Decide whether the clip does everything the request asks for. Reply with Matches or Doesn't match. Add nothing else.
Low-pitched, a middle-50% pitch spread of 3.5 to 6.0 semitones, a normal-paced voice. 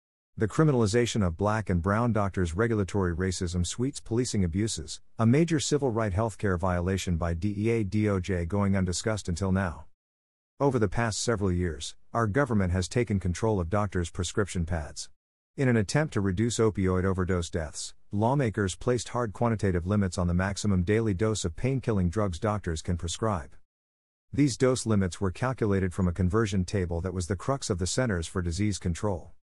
Matches